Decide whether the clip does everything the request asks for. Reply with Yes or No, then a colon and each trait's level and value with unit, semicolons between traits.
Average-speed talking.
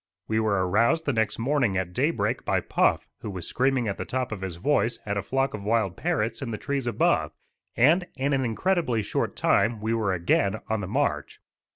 No: fast, 210 wpm